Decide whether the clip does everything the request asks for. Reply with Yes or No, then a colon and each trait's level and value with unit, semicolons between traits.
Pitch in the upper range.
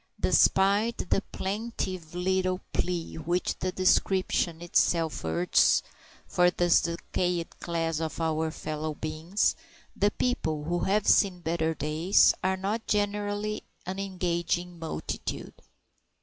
No: medium, 175 Hz